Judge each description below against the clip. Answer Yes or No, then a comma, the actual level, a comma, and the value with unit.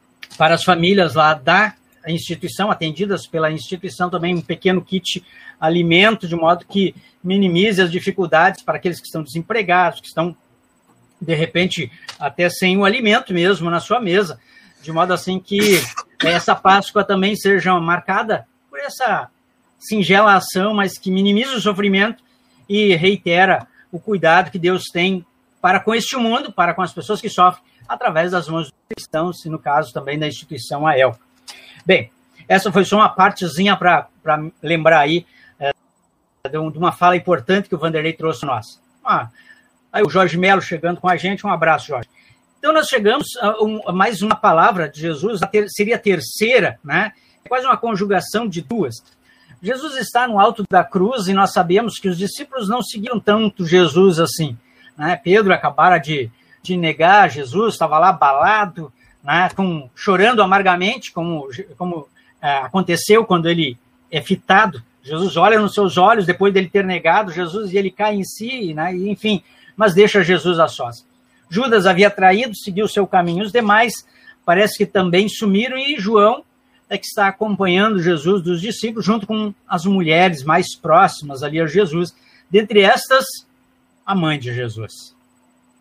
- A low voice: No, medium, 185 Hz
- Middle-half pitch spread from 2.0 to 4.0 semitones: Yes, average, 3.6 semitones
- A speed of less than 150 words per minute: No, average, 170 wpm